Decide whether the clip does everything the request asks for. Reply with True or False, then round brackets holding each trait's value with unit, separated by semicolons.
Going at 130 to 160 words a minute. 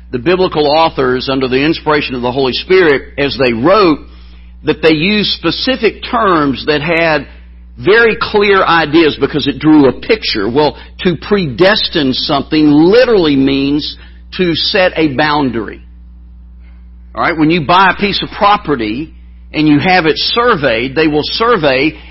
True (150 wpm)